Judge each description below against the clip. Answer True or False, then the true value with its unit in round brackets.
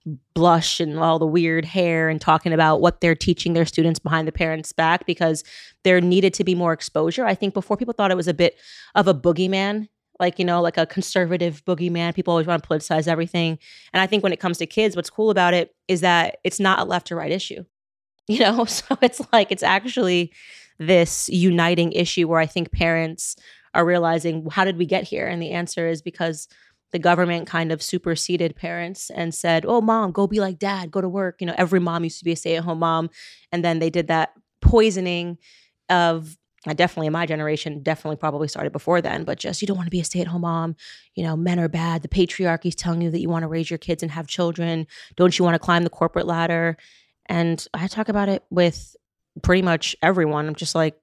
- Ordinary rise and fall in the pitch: False (1.8 semitones)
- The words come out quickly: True (230 wpm)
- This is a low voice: False (170 Hz)